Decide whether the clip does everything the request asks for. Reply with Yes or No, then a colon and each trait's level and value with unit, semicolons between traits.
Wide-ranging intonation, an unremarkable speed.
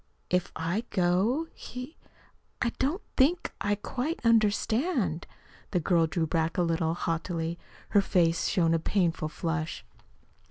No: wide, 5.7 semitones; slow, 130 wpm